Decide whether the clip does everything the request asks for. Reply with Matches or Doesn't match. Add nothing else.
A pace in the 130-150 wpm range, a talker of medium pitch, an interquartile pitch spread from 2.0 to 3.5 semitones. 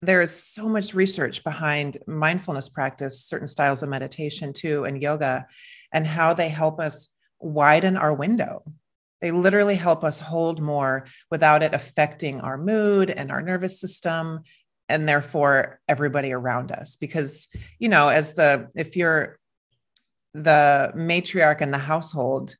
Matches